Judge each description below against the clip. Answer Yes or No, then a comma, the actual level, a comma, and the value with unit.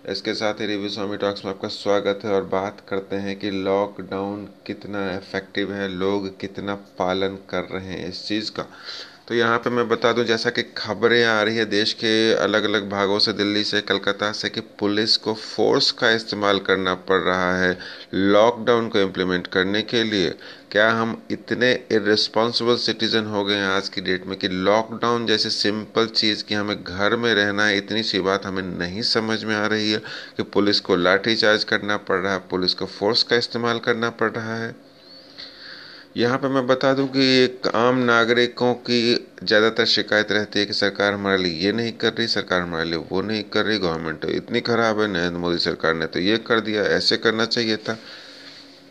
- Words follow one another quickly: Yes, fast, 200 wpm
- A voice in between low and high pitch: No, low, 105 Hz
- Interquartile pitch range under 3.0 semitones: Yes, narrow, 2.5 semitones